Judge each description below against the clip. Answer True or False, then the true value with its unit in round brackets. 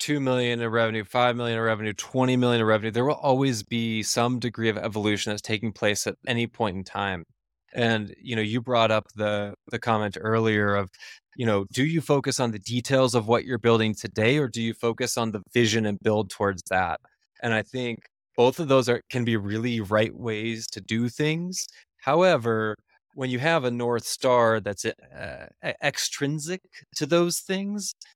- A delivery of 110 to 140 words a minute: False (195 wpm)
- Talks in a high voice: False (115 Hz)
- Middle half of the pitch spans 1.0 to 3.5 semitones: True (2.6 semitones)